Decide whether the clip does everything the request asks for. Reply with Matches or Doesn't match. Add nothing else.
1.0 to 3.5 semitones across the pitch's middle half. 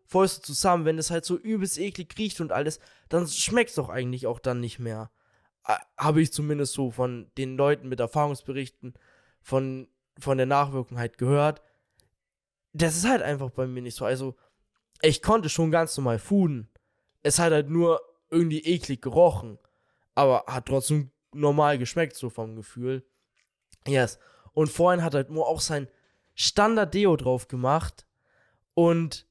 Doesn't match